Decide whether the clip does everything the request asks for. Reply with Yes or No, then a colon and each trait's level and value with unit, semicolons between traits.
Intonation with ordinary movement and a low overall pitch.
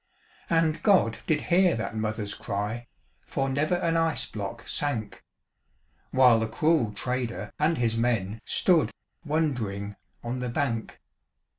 No: wide, 5.8 semitones; low, 120 Hz